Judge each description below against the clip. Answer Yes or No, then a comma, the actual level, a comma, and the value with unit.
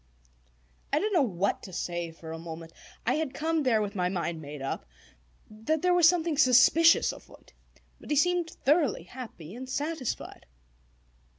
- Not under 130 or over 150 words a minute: No, average, 165 wpm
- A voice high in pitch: Yes, very high, 255 Hz